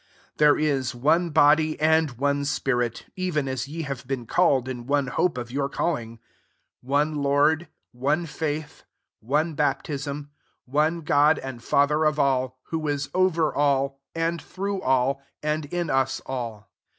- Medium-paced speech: Yes, average, 160 wpm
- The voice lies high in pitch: No, medium, 145 Hz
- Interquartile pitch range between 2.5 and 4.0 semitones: Yes, average, 2.8 semitones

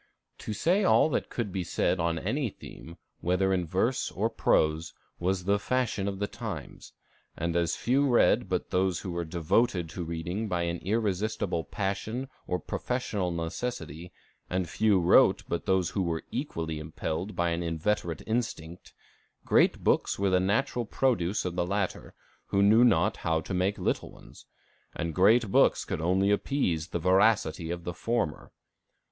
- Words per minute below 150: No, average, 165 wpm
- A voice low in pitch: Yes, very low, 95 Hz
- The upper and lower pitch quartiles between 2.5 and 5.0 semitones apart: Yes, average, 4.1 semitones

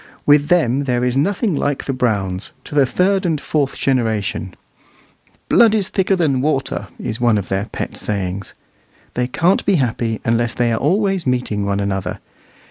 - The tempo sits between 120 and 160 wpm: No, average, 170 wpm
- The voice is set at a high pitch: No, low, 125 Hz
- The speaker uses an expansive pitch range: Yes, wide, 6.2 semitones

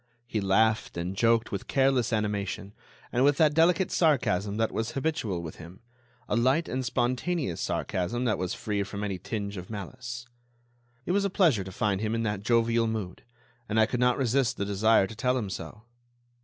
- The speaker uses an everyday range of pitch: Yes, average, 4.0 semitones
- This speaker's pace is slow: No, average, 190 wpm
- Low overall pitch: Yes, low, 115 Hz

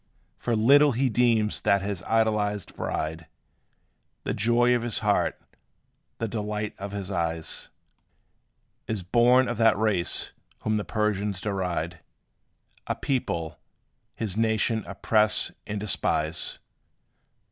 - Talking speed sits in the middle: No, slow, 115 wpm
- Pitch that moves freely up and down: No, average, 2.8 semitones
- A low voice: Yes, low, 105 Hz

